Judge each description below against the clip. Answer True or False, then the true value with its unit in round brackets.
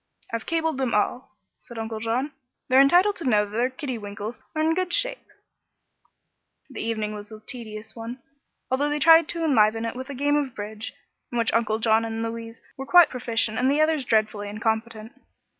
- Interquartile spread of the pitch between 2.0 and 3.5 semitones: False (4.5 semitones)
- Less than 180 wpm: False (190 wpm)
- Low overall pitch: False (235 Hz)